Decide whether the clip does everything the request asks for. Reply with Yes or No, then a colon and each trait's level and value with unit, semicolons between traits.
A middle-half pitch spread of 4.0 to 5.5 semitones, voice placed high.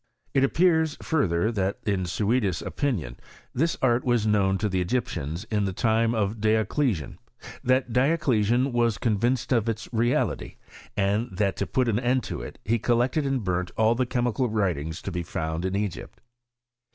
No: average, 4.4 semitones; low, 110 Hz